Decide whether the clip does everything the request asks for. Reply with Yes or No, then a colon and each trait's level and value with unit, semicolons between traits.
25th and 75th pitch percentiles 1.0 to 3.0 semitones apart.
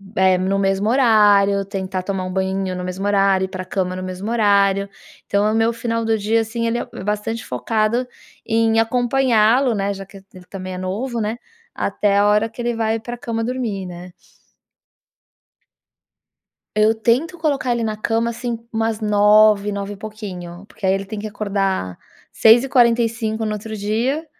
Yes: average, 2.7 semitones